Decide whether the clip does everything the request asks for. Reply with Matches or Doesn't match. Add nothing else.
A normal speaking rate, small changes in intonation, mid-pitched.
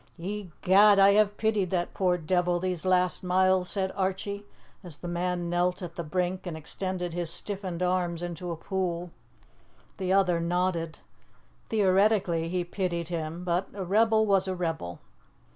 Matches